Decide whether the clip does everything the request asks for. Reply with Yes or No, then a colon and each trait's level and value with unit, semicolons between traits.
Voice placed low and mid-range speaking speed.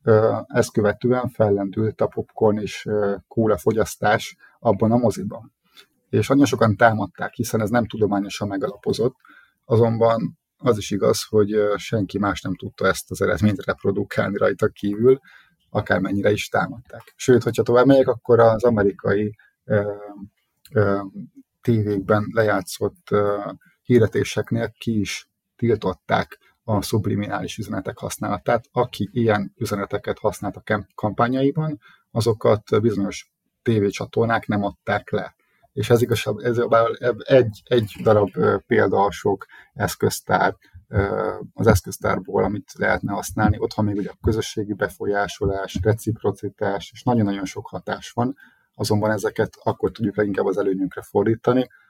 Yes: low, 105 Hz; average, 125 wpm